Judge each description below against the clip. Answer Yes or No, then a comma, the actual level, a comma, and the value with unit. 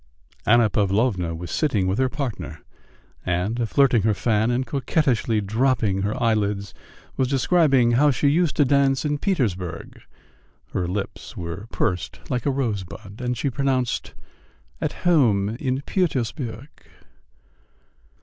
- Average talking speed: No, slow, 130 wpm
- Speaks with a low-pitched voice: Yes, low, 120 Hz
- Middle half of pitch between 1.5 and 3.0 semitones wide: No, average, 5.0 semitones